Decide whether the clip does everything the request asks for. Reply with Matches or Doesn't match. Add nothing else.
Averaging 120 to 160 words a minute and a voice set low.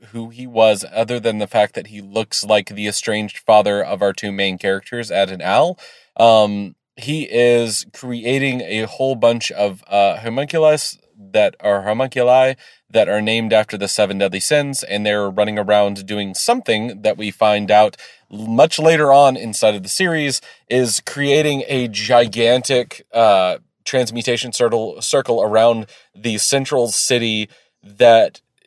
Matches